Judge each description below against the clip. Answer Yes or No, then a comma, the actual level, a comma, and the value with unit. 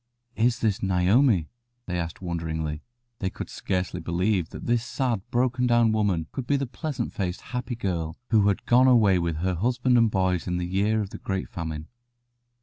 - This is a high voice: No, low, 100 Hz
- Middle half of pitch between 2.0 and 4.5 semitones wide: No, average, 5.2 semitones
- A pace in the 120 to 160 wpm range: No, average, 185 wpm